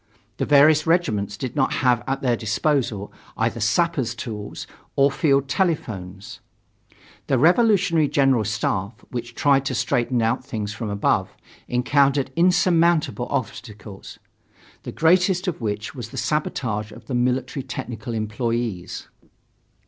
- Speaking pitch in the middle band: No, low, 125 Hz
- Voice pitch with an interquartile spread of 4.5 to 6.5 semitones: Yes, average, 5.2 semitones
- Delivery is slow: Yes, slow, 125 wpm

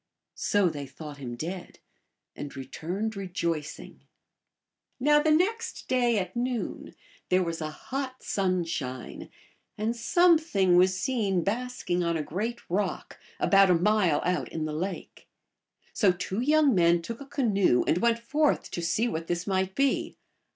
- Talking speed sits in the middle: Yes, average, 155 wpm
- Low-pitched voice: No, high, 190 Hz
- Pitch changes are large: Yes, wide, 6.1 semitones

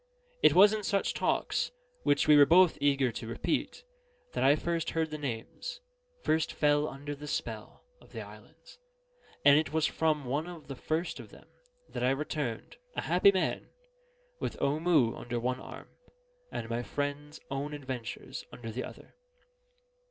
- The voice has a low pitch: No, medium, 145 Hz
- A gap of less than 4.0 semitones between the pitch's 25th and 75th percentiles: Yes, average, 3.5 semitones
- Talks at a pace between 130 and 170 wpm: Yes, average, 165 wpm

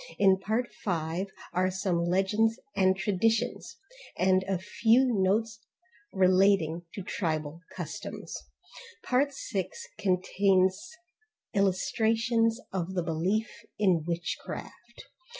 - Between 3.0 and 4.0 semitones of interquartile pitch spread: Yes, average, 3.3 semitones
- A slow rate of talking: Yes, slow, 95 wpm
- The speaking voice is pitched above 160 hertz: Yes, high, 190 Hz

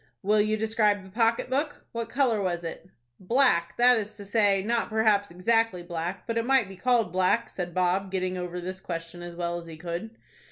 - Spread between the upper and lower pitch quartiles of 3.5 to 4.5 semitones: Yes, average, 4.2 semitones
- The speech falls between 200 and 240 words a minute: Yes, fast, 205 wpm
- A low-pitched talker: No, high, 195 Hz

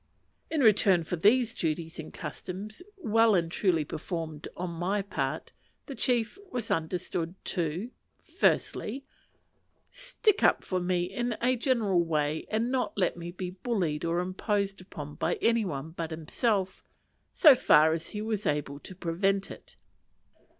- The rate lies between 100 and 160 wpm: Yes, average, 150 wpm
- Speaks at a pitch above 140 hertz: Yes, medium, 185 Hz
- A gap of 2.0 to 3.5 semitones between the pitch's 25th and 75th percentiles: No, average, 5.2 semitones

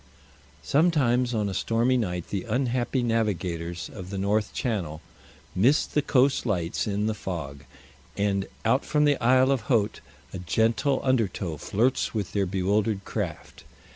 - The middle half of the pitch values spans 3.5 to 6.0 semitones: Yes, average, 4.8 semitones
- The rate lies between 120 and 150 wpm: Yes, average, 145 wpm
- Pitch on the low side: Yes, low, 110 Hz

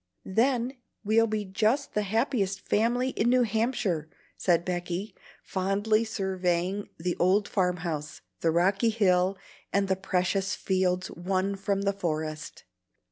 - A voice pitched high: Yes, high, 195 Hz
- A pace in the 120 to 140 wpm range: Yes, slow, 135 wpm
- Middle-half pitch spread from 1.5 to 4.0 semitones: Yes, average, 3.2 semitones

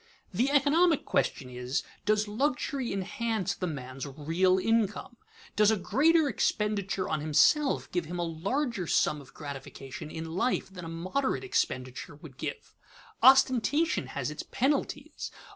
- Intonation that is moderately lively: No, wide, 8.8 semitones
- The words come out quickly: No, average, 145 wpm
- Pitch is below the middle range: No, high, 195 Hz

